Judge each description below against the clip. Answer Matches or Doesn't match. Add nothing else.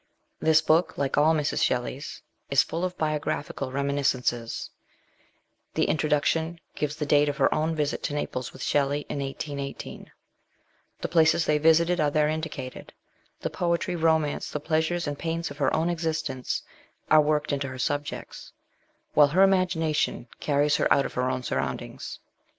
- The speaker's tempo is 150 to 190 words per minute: Matches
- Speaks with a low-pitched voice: Doesn't match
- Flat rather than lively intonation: Matches